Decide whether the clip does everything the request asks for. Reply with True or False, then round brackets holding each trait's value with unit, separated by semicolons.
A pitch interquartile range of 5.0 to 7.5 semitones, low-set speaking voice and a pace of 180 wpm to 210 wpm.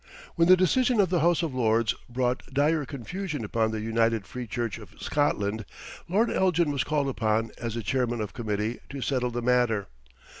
True (5.3 semitones; 125 Hz; 185 wpm)